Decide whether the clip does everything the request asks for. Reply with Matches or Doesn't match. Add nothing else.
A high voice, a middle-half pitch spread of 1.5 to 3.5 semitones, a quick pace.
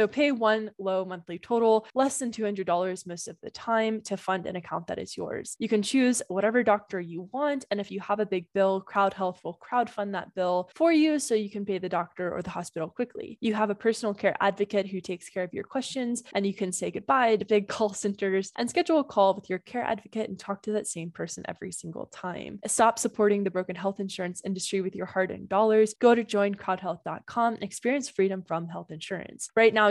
Matches